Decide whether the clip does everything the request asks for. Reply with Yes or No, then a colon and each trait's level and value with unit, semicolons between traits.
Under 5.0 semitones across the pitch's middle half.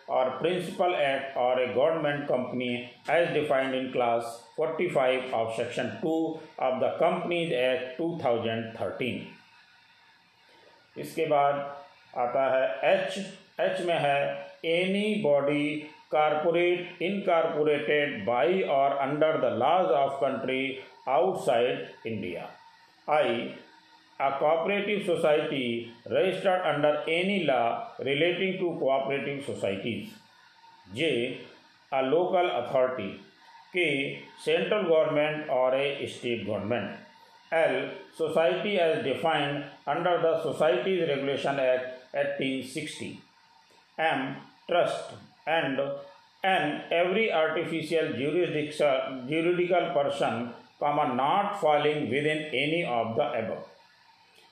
Yes: average, 4.6 semitones